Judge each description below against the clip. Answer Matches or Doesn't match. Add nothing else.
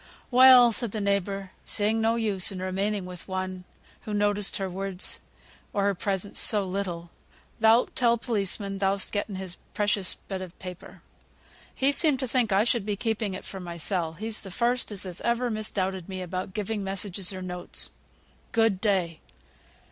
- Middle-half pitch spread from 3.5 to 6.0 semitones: Doesn't match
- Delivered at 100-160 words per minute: Doesn't match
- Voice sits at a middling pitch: Doesn't match